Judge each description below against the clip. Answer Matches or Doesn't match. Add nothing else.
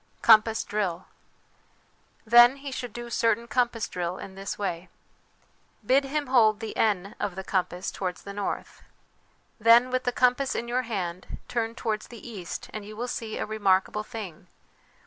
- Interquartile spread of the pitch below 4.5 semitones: Matches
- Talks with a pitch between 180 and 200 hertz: Doesn't match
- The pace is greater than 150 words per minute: Matches